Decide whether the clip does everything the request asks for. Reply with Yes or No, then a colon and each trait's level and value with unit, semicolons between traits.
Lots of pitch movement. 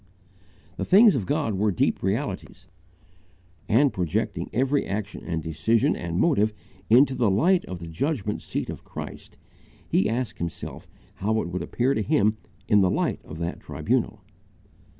Yes: wide, 5.8 semitones